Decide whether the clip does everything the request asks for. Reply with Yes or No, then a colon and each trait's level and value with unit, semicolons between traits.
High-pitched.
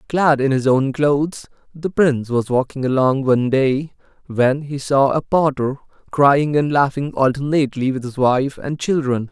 No: low, 135 Hz